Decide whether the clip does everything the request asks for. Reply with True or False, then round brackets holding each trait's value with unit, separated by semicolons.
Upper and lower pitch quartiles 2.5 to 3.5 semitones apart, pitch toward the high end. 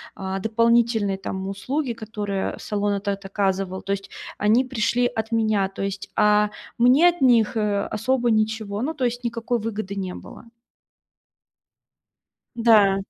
True (3.0 semitones; 215 Hz)